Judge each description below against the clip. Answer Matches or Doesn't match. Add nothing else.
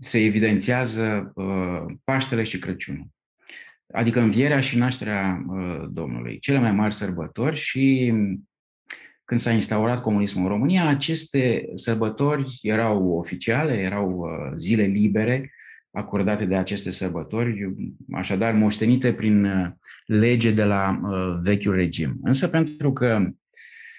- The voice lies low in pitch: Matches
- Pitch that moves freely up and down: Doesn't match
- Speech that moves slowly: Matches